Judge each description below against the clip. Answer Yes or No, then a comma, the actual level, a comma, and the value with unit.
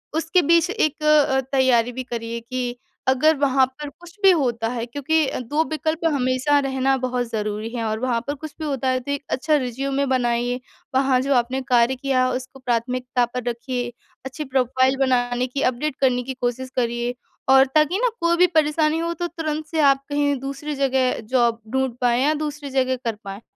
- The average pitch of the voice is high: Yes, very high, 260 Hz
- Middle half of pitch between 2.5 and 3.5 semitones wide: Yes, average, 2.9 semitones